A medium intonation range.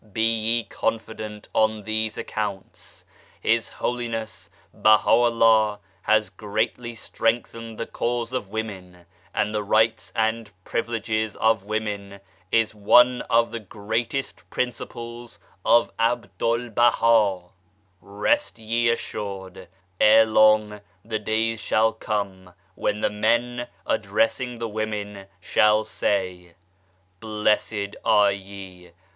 No: narrow, 2.0 semitones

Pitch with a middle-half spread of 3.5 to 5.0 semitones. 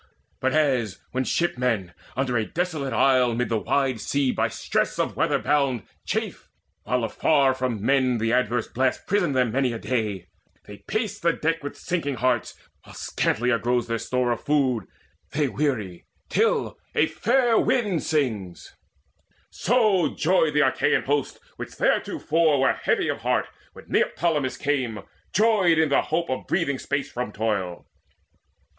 Yes: average, 4.7 semitones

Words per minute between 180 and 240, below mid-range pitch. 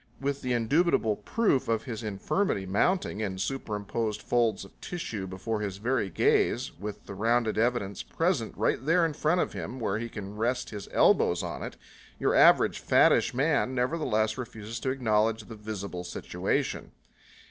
No: average, 160 wpm; low, 115 Hz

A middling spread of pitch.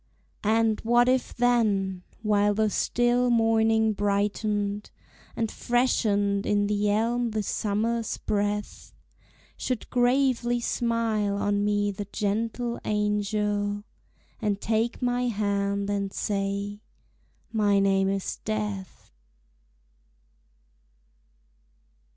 No: narrow, 2.2 semitones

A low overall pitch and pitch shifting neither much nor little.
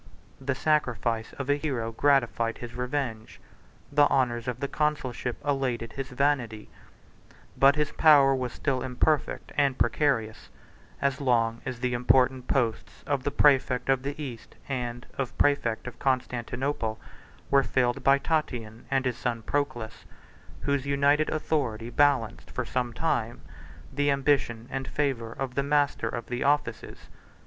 Yes: low, 130 Hz; average, 3.1 semitones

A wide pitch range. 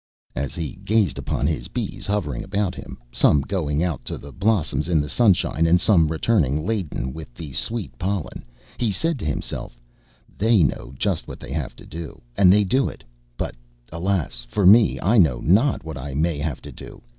Yes: wide, 5.7 semitones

